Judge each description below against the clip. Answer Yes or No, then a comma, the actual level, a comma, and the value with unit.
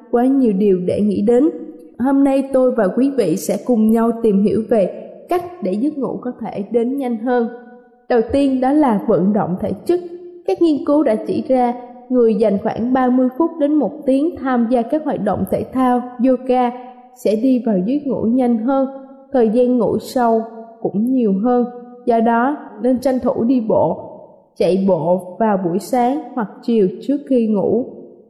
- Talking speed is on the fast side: No, average, 185 wpm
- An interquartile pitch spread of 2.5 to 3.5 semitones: Yes, average, 3.1 semitones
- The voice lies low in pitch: No, high, 245 Hz